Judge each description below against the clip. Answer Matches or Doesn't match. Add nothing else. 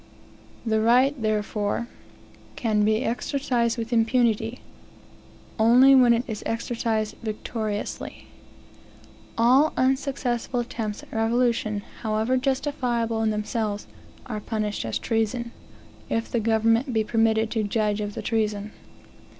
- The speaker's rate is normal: Doesn't match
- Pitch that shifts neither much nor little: Doesn't match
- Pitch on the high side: Matches